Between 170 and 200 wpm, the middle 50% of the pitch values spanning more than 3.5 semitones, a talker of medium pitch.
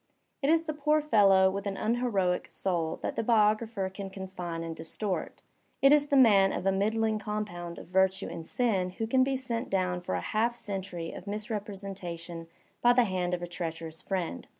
No: average, 195 wpm; average, 4.0 semitones; high, 195 Hz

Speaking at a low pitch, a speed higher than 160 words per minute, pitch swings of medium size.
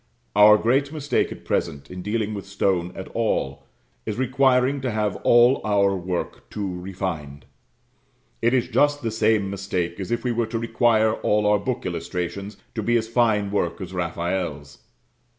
Yes: low, 105 Hz; average, 170 wpm; average, 4.0 semitones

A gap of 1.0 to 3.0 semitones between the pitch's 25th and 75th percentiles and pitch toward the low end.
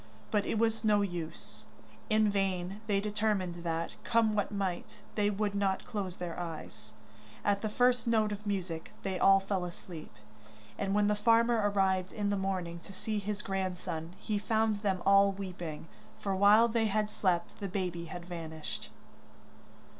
No: average, 2.7 semitones; high, 200 Hz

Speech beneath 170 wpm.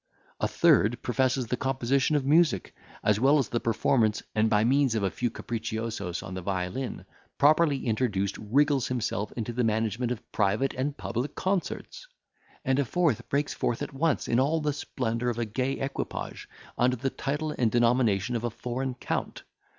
No: average, 175 wpm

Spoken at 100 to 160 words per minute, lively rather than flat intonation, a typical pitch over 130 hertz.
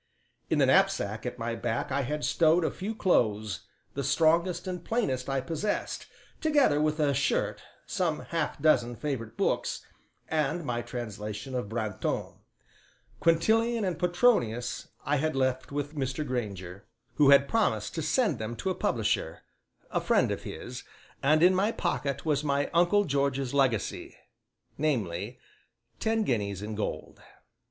Yes: average, 145 wpm; wide, 5.9 semitones; medium, 140 Hz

